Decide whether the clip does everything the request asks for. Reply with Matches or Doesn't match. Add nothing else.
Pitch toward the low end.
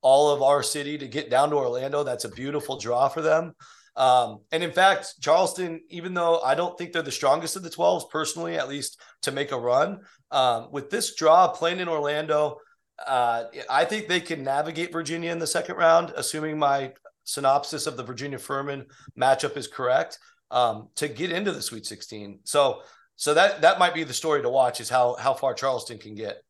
Doesn't match